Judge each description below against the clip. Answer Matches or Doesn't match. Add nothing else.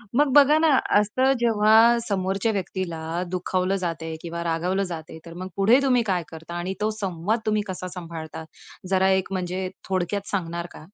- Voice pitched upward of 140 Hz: Matches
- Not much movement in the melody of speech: Doesn't match